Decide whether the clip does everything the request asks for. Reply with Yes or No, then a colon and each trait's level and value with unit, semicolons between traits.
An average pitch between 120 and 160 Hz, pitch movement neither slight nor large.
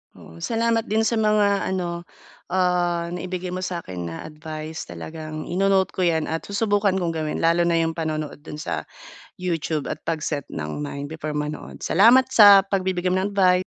No: medium, 175 Hz; average, 3.7 semitones